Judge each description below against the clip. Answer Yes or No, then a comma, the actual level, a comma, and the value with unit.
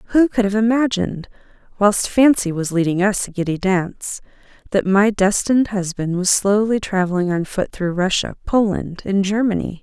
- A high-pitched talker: Yes, high, 200 Hz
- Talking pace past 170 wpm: No, average, 160 wpm